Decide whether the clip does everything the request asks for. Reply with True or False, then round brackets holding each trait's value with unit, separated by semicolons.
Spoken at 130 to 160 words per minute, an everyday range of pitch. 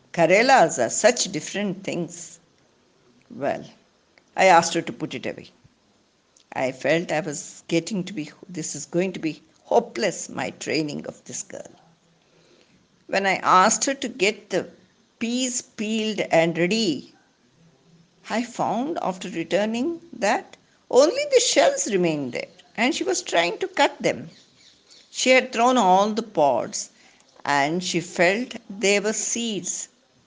False (140 wpm; 5.9 semitones)